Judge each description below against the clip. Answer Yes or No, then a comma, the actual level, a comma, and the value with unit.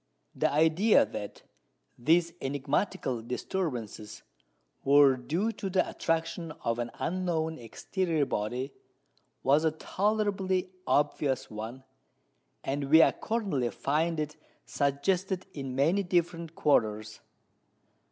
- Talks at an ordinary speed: No, slow, 105 wpm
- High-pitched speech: No, medium, 155 Hz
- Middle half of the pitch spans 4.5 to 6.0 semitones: Yes, average, 5.2 semitones